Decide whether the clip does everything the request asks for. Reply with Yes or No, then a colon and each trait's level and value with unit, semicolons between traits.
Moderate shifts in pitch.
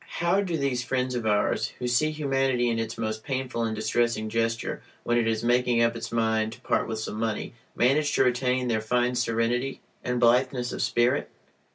No: narrow, 2.0 semitones